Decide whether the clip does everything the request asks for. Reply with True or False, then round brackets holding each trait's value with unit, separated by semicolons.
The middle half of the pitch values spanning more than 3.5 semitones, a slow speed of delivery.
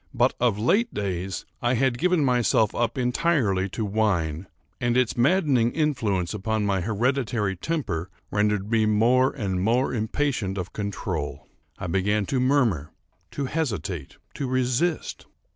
True (4.9 semitones; 130 wpm)